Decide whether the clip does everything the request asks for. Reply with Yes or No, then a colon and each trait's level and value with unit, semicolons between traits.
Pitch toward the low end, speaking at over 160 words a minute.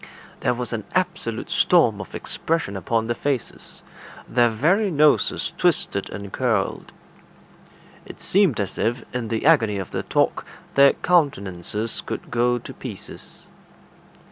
No: low, 120 Hz; slow, 135 wpm